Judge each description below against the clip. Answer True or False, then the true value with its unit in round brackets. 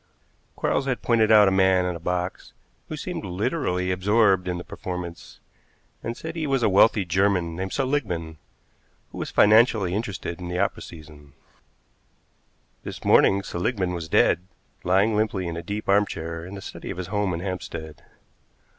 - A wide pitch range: False (3.2 semitones)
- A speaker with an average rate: True (170 wpm)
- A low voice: True (95 Hz)